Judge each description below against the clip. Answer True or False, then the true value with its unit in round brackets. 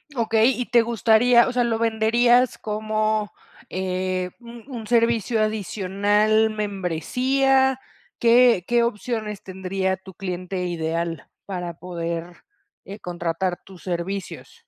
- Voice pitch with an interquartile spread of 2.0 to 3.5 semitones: False (4.3 semitones)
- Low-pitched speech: False (210 Hz)